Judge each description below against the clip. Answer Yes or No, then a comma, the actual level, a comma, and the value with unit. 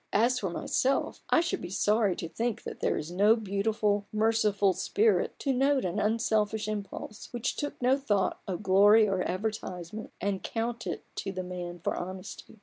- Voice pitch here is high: Yes, high, 210 Hz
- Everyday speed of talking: Yes, average, 175 wpm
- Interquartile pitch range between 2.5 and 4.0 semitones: Yes, average, 3.1 semitones